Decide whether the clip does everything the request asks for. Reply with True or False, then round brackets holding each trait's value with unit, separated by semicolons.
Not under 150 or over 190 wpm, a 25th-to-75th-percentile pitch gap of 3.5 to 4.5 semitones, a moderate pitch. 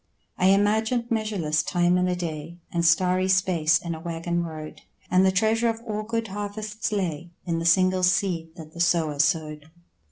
True (180 wpm; 3.8 semitones; 180 Hz)